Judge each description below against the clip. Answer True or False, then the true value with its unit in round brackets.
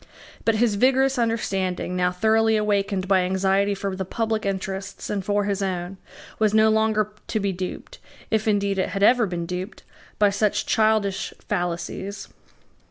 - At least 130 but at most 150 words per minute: False (160 wpm)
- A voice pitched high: True (200 Hz)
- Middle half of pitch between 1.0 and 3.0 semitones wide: True (2.4 semitones)